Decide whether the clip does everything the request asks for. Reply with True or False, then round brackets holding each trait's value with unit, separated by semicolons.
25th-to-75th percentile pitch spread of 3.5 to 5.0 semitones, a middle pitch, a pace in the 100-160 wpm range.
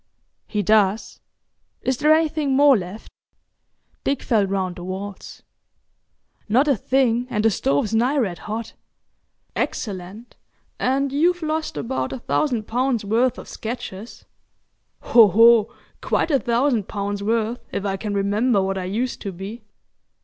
False (4.4 semitones; 225 Hz; 140 wpm)